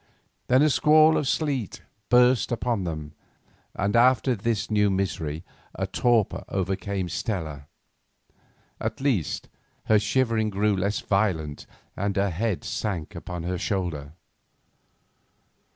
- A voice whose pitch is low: Yes, low, 100 Hz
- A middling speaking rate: No, slow, 120 wpm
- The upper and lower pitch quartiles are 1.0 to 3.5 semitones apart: No, average, 4.9 semitones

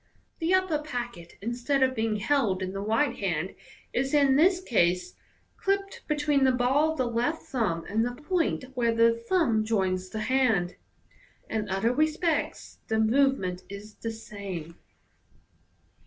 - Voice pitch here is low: No, high, 235 Hz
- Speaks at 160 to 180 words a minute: No, average, 150 wpm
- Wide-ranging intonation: Yes, wide, 6.1 semitones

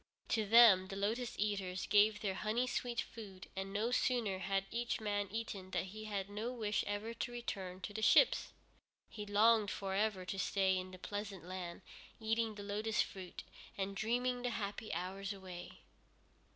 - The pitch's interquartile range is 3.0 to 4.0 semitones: No, narrow, 2.6 semitones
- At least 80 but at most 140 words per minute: No, average, 175 wpm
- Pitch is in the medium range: No, high, 205 Hz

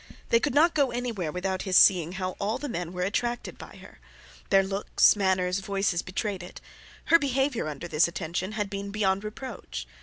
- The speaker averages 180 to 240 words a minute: Yes, average, 185 wpm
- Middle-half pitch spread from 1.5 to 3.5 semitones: No, average, 4.1 semitones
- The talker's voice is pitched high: Yes, high, 195 Hz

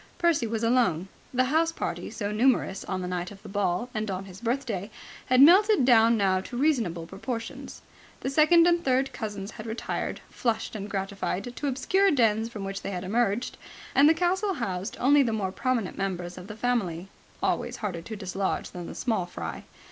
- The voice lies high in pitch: Yes, high, 220 Hz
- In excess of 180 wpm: Yes, average, 190 wpm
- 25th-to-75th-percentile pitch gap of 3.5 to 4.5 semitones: No, average, 5.0 semitones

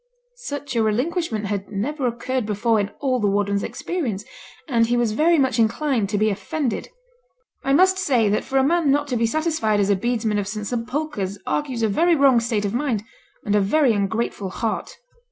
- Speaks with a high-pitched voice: Yes, high, 235 Hz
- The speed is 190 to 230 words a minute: Yes, average, 195 wpm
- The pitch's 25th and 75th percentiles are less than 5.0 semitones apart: No, average, 5.3 semitones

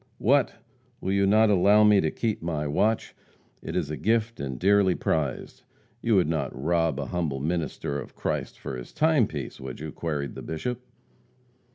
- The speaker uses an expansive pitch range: Yes, wide, 6.4 semitones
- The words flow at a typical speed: Yes, average, 175 wpm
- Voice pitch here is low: Yes, very low, 85 Hz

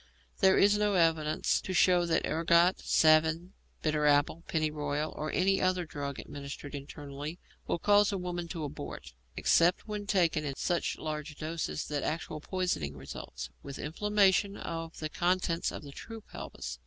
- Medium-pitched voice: Yes, medium, 165 Hz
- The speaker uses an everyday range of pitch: Yes, average, 3.5 semitones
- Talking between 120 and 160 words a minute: Yes, average, 155 wpm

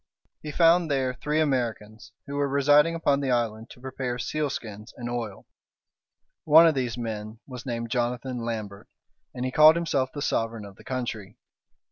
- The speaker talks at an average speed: Yes, average, 165 wpm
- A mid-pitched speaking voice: No, low, 125 Hz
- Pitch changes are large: No, average, 3.8 semitones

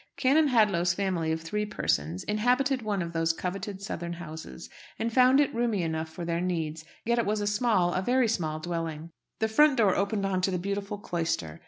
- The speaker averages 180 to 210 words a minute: Yes, average, 200 wpm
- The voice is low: No, high, 190 Hz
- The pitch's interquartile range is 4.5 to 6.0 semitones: Yes, average, 4.8 semitones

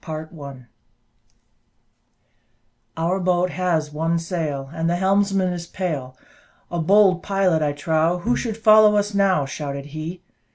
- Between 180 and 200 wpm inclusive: No, slow, 135 wpm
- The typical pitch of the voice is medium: Yes, medium, 170 Hz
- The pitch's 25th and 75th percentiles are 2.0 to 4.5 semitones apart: Yes, average, 3.6 semitones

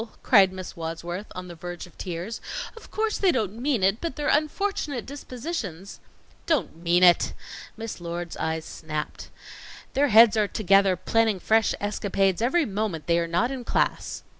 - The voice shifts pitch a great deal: Yes, wide, 5.9 semitones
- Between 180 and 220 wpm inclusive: No, average, 165 wpm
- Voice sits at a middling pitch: No, high, 200 Hz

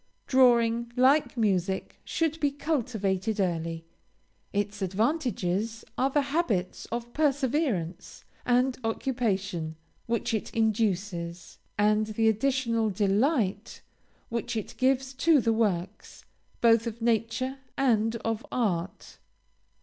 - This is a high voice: Yes, high, 225 Hz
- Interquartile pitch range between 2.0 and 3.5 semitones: No, average, 4.5 semitones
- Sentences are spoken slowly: Yes, slow, 105 wpm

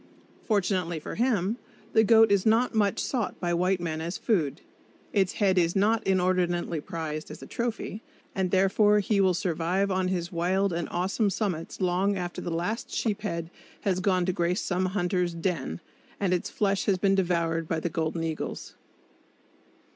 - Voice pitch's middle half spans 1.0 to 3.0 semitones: Yes, narrow, 2.6 semitones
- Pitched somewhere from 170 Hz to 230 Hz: Yes, medium, 185 Hz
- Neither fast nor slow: Yes, average, 170 wpm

